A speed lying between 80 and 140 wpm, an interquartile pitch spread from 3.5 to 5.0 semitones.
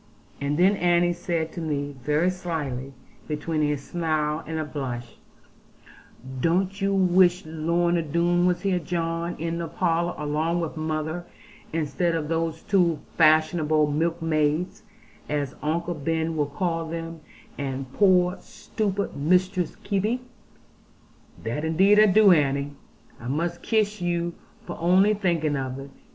No: slow, 135 wpm; average, 2.8 semitones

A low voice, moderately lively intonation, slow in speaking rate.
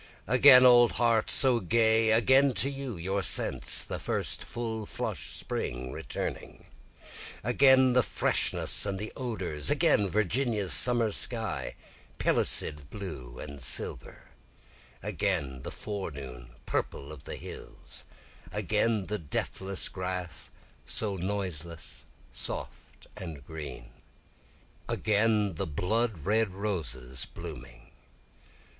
No: low, 100 Hz; wide, 6.9 semitones; slow, 105 wpm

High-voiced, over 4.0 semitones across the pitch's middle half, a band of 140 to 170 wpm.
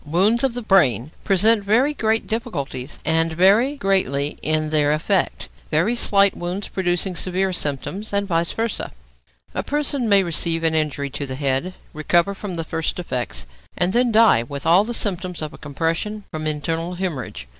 No: medium, 175 Hz; average, 5.0 semitones; average, 165 wpm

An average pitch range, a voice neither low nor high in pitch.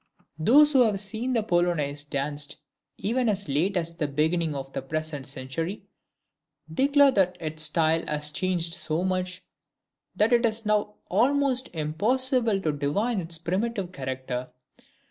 No: wide, 6.3 semitones; medium, 175 Hz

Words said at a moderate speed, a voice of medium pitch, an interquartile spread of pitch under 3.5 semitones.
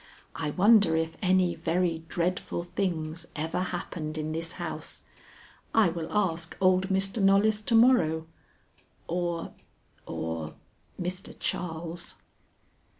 No: slow, 110 wpm; medium, 175 Hz; average, 2.8 semitones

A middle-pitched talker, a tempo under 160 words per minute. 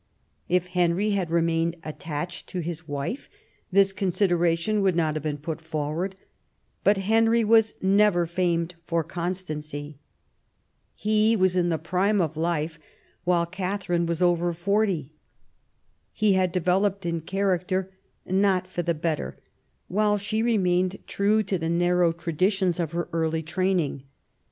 Yes: medium, 180 Hz; average, 140 wpm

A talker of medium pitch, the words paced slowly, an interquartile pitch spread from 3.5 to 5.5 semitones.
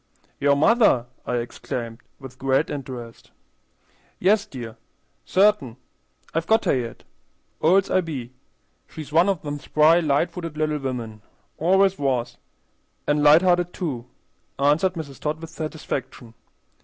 Yes: medium, 150 Hz; slow, 130 wpm; average, 5.0 semitones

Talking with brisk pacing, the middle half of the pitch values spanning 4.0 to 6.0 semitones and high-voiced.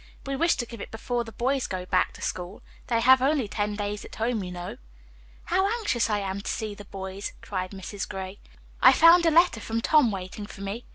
Yes: fast, 225 wpm; average, 4.6 semitones; high, 215 Hz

